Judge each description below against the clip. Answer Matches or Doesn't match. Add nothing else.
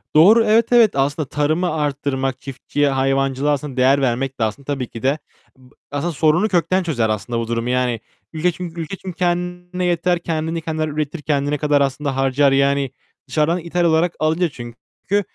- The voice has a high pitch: Doesn't match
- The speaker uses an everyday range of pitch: Matches